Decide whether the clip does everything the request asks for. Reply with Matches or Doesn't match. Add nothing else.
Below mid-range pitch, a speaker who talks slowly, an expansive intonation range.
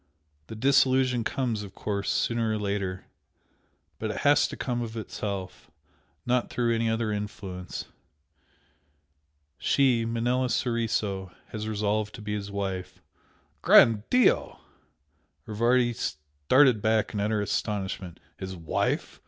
Doesn't match